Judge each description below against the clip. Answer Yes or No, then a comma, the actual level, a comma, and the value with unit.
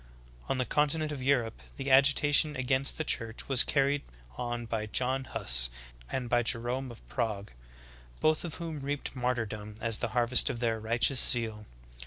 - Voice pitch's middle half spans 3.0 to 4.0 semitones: Yes, average, 3.3 semitones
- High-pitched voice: No, low, 125 Hz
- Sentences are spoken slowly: No, average, 170 wpm